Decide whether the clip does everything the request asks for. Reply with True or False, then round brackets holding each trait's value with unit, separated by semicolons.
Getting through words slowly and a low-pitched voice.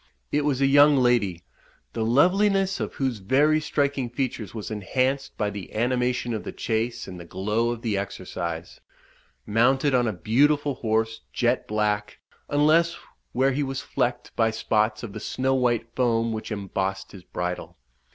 False (160 wpm; 120 Hz)